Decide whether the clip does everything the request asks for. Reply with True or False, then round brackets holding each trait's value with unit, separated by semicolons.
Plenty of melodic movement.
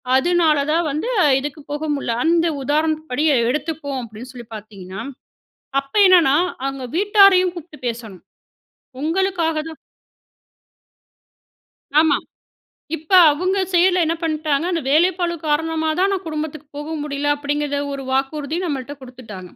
False (3.6 semitones)